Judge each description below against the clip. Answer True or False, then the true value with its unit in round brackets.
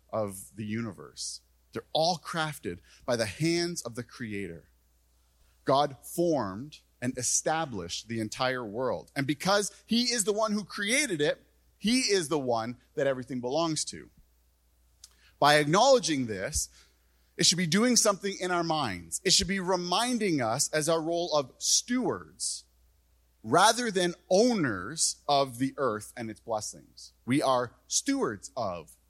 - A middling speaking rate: True (145 wpm)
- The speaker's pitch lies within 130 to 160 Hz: True (135 Hz)